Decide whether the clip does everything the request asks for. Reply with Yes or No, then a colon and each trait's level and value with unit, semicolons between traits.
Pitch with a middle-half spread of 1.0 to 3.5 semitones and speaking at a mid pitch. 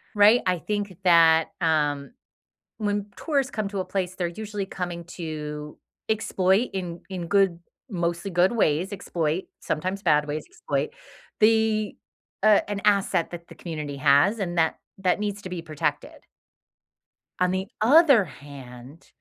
No: average, 4.3 semitones; medium, 180 Hz